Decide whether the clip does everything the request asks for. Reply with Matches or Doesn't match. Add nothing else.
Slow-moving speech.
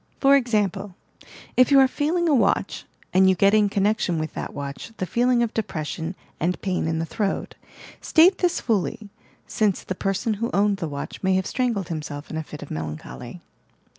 Doesn't match